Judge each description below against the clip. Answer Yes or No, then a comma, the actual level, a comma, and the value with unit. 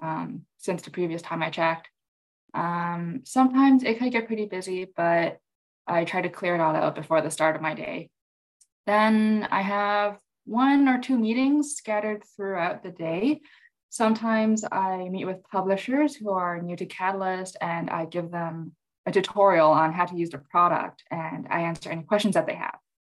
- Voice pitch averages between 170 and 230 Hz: Yes, medium, 185 Hz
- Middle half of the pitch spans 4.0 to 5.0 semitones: Yes, average, 4.5 semitones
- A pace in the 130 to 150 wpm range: No, average, 180 wpm